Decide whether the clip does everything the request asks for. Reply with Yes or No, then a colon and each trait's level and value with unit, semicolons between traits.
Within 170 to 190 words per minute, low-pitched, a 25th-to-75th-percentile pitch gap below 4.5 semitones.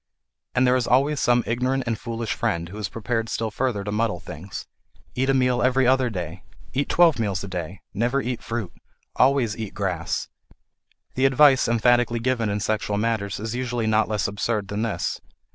Yes: average, 185 wpm; low, 115 Hz; average, 3.6 semitones